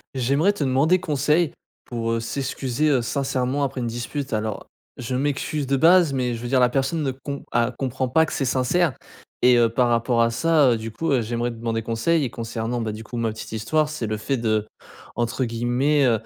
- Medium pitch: No, low, 125 Hz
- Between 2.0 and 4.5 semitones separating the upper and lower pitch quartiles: Yes, average, 3.5 semitones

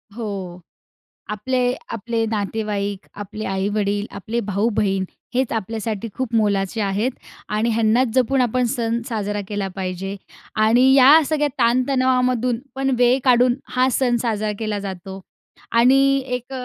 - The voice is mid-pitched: No, high, 225 Hz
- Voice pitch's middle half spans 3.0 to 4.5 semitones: Yes, average, 3.5 semitones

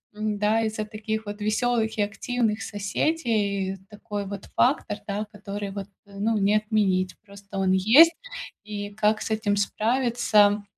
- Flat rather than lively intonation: Yes, narrow, 1.4 semitones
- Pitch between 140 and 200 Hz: No, high, 210 Hz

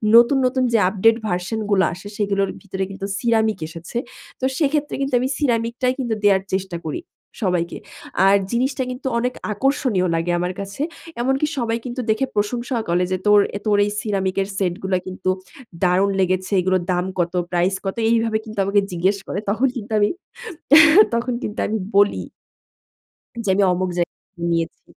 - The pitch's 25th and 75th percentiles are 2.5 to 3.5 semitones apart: No, average, 4.1 semitones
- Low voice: No, high, 205 Hz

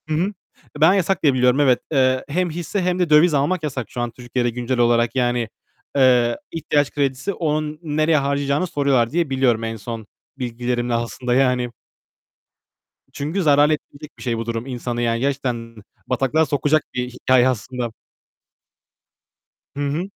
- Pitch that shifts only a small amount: No, average, 3.8 semitones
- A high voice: No, low, 130 Hz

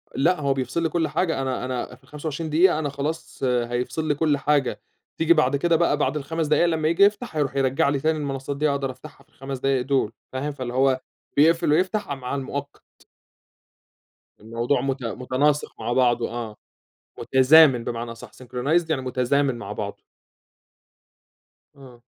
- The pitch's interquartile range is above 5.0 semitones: No, average, 3.3 semitones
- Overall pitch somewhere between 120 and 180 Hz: Yes, medium, 140 Hz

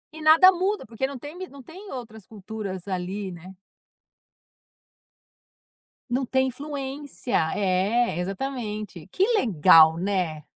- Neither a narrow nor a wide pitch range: No, wide, 6.7 semitones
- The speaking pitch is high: Yes, high, 220 Hz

